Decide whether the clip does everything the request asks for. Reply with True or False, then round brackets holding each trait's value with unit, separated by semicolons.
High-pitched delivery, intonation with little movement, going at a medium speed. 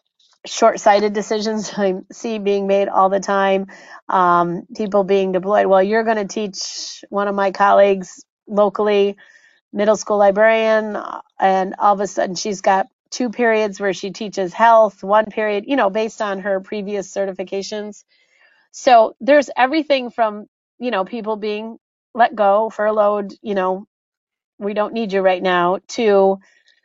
True (210 Hz; 2.2 semitones; 155 wpm)